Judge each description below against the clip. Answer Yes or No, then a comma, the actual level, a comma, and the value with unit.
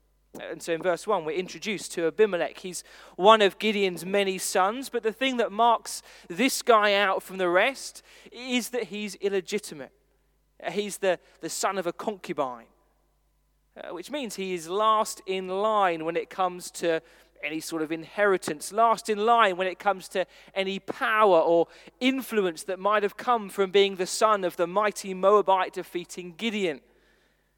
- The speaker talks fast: No, average, 170 wpm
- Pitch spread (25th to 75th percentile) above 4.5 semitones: No, average, 3.5 semitones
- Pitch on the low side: No, high, 190 Hz